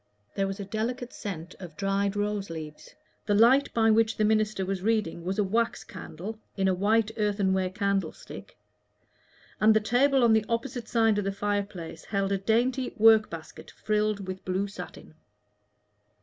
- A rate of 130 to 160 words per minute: No, average, 170 wpm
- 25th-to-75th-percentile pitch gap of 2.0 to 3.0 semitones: Yes, narrow, 2.5 semitones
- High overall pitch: Yes, high, 205 Hz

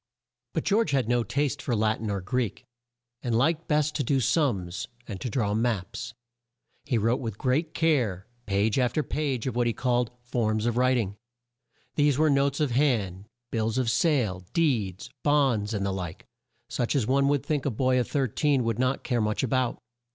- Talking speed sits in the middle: Yes, average, 190 wpm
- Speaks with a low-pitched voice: Yes, low, 125 Hz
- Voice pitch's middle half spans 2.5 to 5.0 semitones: Yes, average, 4.3 semitones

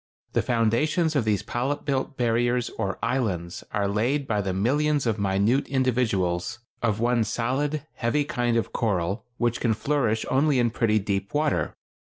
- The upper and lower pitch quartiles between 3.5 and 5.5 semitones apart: Yes, average, 4.1 semitones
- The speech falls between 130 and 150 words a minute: No, average, 160 wpm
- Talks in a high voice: No, low, 120 Hz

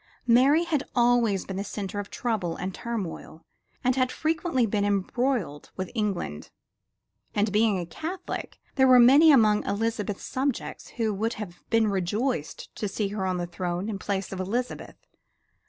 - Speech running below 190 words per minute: Yes, average, 160 wpm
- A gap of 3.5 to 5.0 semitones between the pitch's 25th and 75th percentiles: Yes, average, 4.4 semitones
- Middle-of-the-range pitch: No, high, 210 Hz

